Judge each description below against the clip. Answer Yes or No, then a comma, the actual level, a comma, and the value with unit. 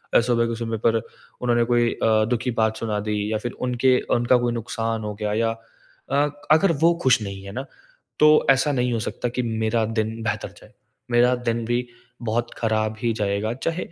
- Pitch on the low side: Yes, low, 115 Hz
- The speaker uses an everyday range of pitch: No, narrow, 2.0 semitones